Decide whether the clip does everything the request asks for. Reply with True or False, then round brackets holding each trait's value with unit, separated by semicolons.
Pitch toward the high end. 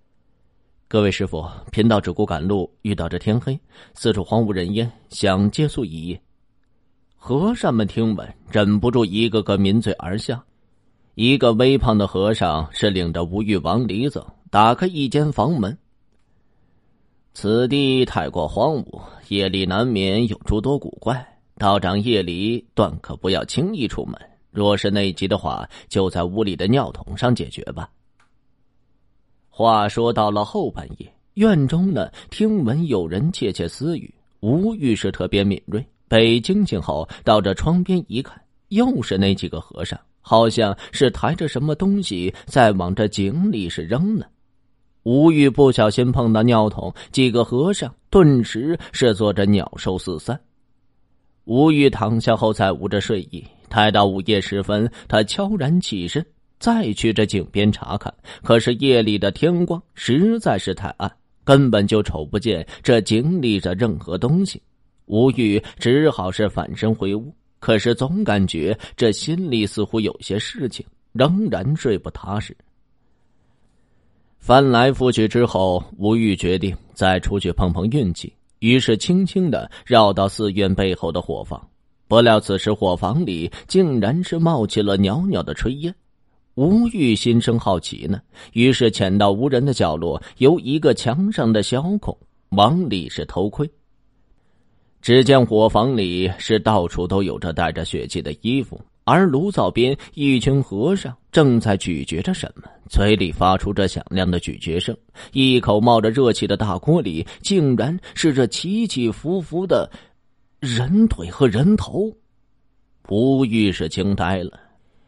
False (110 Hz)